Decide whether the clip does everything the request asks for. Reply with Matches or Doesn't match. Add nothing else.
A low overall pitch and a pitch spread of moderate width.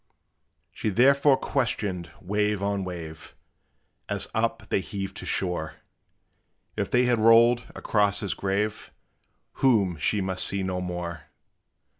Matches